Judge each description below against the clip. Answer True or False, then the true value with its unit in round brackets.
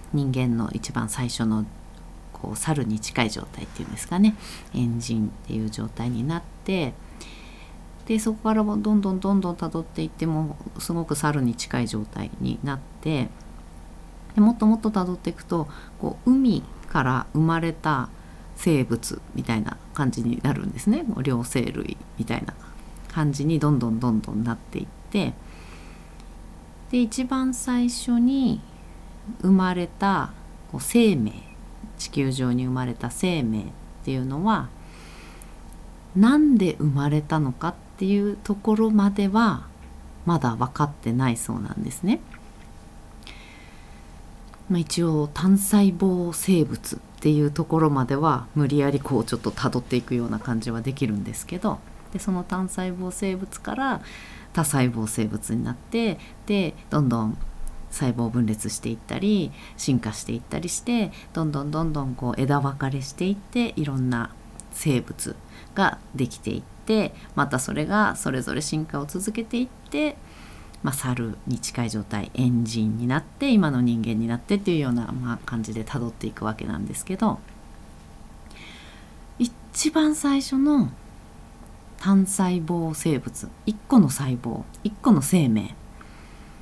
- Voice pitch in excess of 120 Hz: True (140 Hz)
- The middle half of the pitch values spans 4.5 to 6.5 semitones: False (8.8 semitones)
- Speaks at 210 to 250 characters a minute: False (285 characters per minute)